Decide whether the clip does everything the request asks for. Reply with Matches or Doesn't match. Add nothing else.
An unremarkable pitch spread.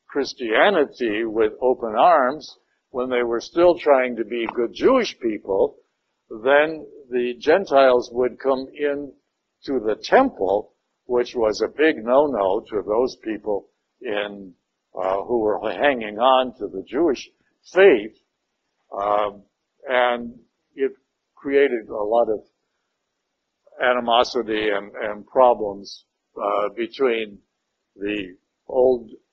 Matches